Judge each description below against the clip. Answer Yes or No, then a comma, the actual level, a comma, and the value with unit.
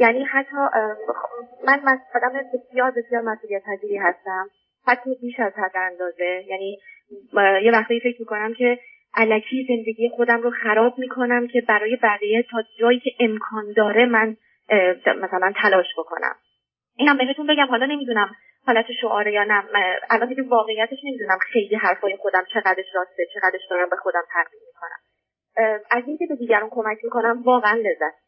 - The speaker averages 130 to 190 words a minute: Yes, fast, 155 wpm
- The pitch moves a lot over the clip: No, average, 3.4 semitones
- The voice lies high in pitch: Yes, high, 225 Hz